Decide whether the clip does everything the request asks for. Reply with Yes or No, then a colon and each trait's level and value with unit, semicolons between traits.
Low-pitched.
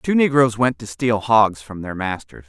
Yes: low, 110 Hz